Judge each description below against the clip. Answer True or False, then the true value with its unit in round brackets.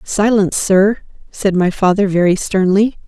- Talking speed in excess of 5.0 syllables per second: False (4.7 syllables/s)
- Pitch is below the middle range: False (195 Hz)